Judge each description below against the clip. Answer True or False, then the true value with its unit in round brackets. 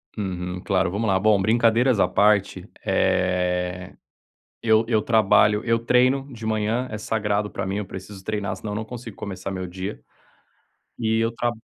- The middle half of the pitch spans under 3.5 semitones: True (3.1 semitones)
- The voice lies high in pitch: False (105 Hz)